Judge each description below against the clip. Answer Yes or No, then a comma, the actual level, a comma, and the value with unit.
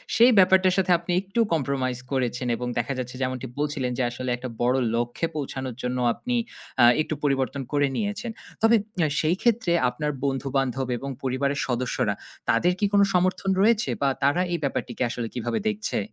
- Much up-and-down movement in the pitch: Yes, wide, 6.4 semitones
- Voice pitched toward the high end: No, medium, 140 Hz